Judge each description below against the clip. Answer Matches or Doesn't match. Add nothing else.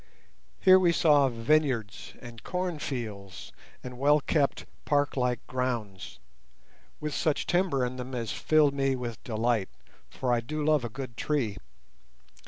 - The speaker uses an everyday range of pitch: Matches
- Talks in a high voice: Doesn't match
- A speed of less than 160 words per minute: Matches